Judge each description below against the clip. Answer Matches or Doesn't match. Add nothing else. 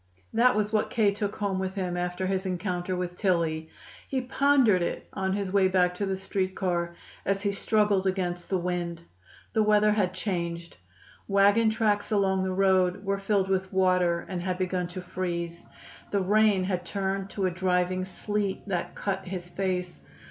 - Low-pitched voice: Doesn't match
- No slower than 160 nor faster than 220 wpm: Matches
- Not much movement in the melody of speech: Matches